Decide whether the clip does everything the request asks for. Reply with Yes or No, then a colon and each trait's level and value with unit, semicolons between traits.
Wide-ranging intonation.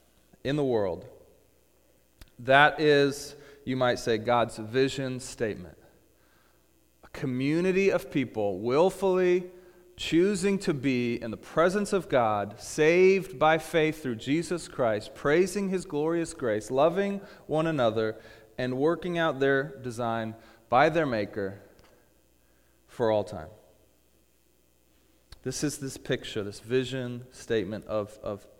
Yes: wide, 6.6 semitones